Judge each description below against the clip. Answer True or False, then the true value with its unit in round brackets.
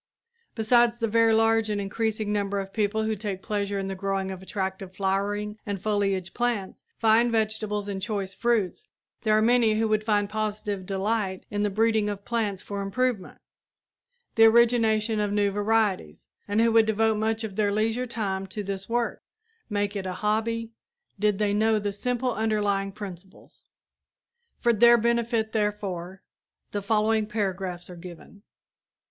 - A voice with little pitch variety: True (2.1 semitones)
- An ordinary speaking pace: True (160 wpm)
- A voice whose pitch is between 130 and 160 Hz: False (210 Hz)